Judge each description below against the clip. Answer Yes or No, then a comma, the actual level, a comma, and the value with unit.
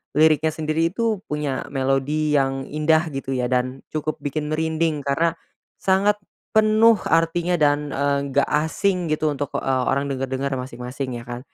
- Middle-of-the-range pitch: Yes, medium, 150 Hz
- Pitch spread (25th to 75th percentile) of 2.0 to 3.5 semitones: Yes, average, 3.0 semitones